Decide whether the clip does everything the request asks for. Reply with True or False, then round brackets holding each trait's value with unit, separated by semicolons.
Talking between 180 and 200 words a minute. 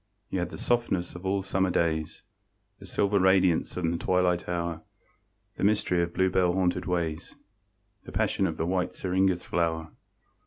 False (160 wpm)